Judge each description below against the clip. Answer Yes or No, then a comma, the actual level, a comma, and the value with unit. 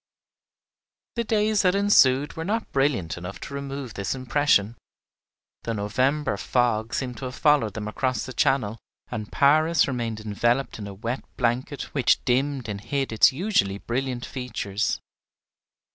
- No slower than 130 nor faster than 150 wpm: Yes, average, 145 wpm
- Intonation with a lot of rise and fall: No, average, 4.6 semitones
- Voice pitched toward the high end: No, low, 130 Hz